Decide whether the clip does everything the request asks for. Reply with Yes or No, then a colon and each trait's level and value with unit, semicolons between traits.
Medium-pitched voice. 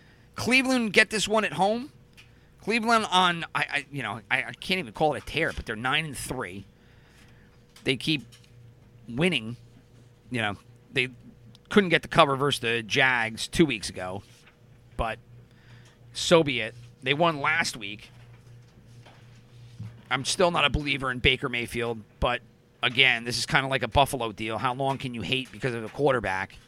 No: low, 120 Hz